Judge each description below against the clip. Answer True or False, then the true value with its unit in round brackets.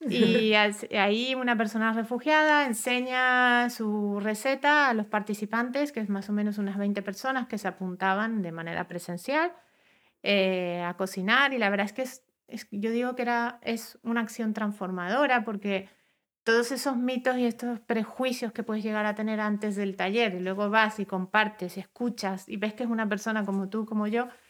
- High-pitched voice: True (220 Hz)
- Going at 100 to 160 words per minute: False (185 wpm)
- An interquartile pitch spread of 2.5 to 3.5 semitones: True (3.1 semitones)